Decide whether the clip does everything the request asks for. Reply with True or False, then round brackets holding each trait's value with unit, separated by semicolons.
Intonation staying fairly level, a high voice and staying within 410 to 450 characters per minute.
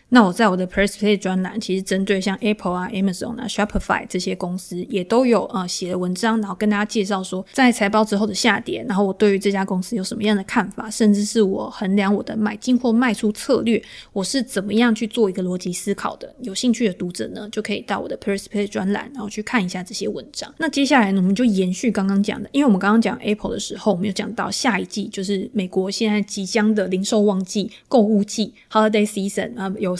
True (2.3 semitones; 205 Hz; 440 characters per minute)